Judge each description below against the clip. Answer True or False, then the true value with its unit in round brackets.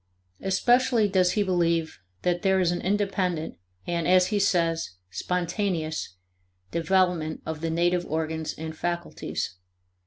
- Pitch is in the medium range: True (175 Hz)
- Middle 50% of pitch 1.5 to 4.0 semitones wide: True (2.7 semitones)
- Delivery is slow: True (125 wpm)